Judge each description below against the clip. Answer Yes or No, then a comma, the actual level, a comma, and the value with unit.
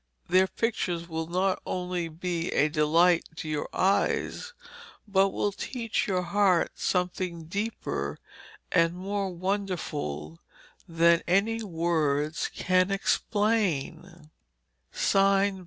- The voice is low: No, medium, 180 Hz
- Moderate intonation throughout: Yes, average, 3.0 semitones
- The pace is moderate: No, slow, 100 wpm